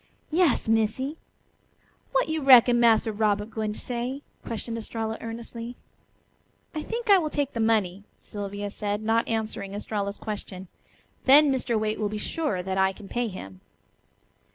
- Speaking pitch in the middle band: No, high, 225 Hz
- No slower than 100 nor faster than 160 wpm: Yes, average, 155 wpm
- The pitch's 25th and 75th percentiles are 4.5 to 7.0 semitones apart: No, average, 3.3 semitones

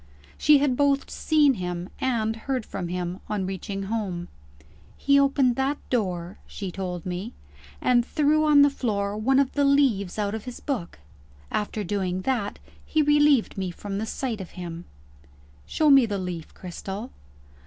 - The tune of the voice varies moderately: No, wide, 6.6 semitones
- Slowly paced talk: No, average, 165 wpm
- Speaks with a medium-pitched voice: No, high, 215 Hz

